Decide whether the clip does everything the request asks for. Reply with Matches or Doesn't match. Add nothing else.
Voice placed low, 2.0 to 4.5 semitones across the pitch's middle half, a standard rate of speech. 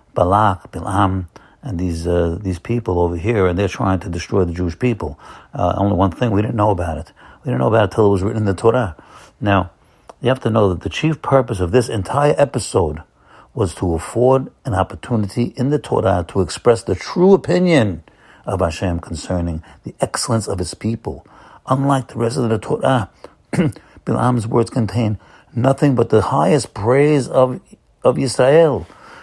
Doesn't match